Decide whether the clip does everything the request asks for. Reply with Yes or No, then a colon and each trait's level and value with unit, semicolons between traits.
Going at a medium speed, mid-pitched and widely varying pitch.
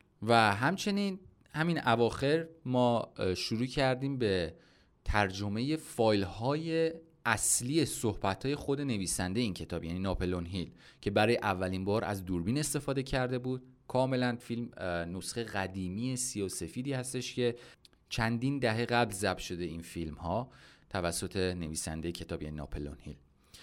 No: average, 135 wpm; low, 110 Hz; wide, 5.9 semitones